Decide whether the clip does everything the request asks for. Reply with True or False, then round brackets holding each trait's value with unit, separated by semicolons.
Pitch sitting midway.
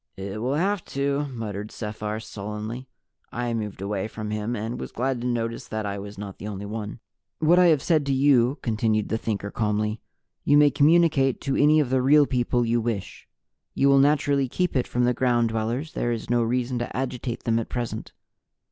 False (120 Hz)